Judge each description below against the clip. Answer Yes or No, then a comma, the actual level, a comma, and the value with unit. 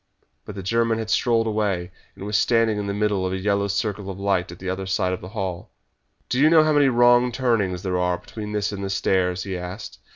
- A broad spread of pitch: No, average, 3.3 semitones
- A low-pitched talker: Yes, low, 100 Hz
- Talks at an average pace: No, fast, 240 wpm